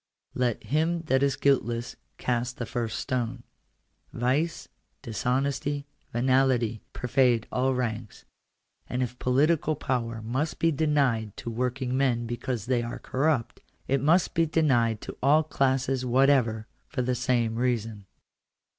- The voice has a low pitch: Yes, low, 125 Hz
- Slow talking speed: Yes, slow, 130 wpm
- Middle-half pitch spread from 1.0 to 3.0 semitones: Yes, narrow, 2.6 semitones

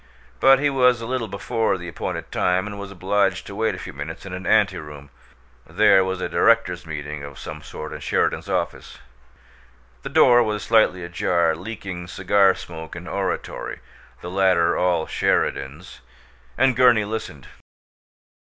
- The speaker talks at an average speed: Yes, average, 155 wpm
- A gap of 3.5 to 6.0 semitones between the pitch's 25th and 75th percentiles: Yes, average, 4.2 semitones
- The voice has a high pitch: No, very low, 95 Hz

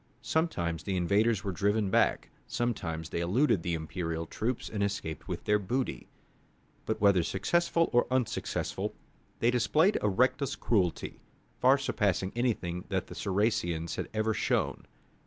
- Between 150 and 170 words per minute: No, average, 140 wpm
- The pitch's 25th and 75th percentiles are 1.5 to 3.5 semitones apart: No, wide, 5.6 semitones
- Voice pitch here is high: No, low, 105 Hz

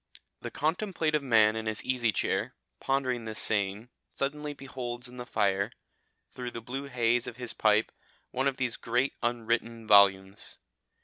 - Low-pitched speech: Yes, low, 120 Hz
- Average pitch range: Yes, average, 3.1 semitones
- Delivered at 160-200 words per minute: No, average, 150 wpm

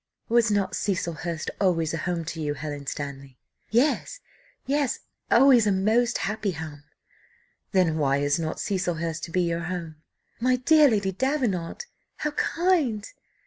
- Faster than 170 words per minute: No, average, 145 wpm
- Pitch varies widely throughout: Yes, wide, 6.7 semitones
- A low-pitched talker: No, medium, 185 Hz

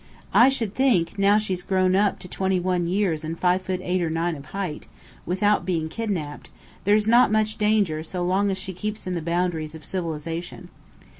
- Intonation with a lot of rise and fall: No, average, 3.3 semitones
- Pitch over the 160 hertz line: Yes, medium, 185 Hz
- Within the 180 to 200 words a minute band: Yes, average, 195 wpm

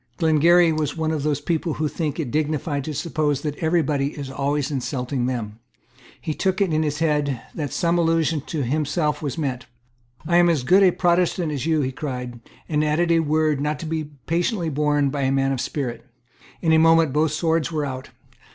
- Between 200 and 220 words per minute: Yes, fast, 205 wpm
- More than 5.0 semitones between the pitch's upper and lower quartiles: No, narrow, 2.5 semitones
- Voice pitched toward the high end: No, medium, 150 Hz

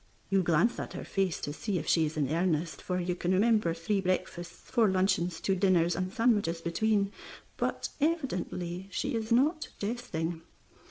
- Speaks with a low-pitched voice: No, medium, 185 Hz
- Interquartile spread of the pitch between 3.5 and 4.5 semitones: Yes, average, 4.1 semitones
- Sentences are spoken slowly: No, average, 170 wpm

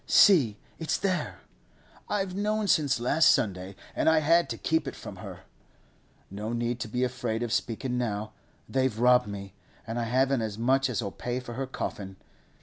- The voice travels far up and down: No, average, 4.1 semitones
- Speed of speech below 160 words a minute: No, average, 175 wpm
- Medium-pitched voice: No, low, 125 Hz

